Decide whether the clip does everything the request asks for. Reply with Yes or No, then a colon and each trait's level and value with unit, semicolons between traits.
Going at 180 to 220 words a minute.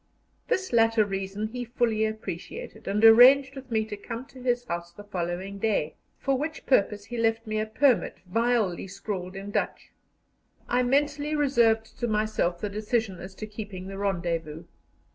No: average, 165 wpm